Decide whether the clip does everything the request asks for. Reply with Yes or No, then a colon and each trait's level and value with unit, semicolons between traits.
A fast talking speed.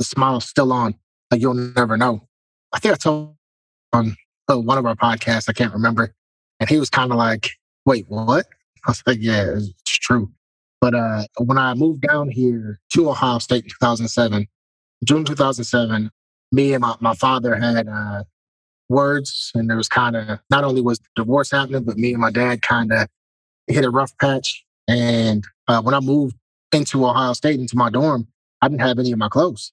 No: average, 195 wpm